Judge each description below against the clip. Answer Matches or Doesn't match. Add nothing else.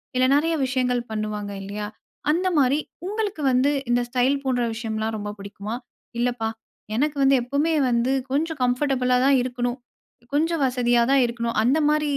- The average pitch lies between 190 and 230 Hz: Doesn't match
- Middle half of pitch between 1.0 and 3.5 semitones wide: Matches